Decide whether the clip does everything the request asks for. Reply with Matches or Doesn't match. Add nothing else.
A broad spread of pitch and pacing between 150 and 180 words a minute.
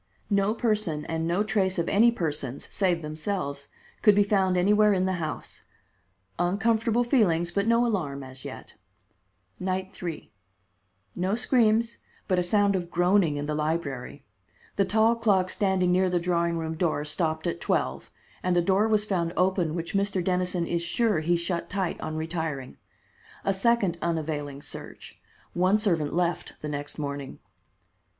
Doesn't match